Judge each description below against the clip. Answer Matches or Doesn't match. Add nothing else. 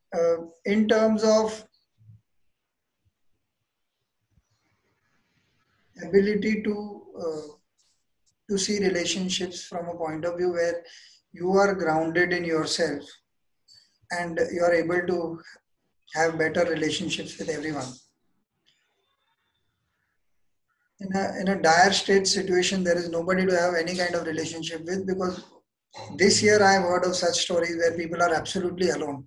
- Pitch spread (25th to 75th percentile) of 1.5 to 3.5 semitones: Matches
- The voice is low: Doesn't match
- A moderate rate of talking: Doesn't match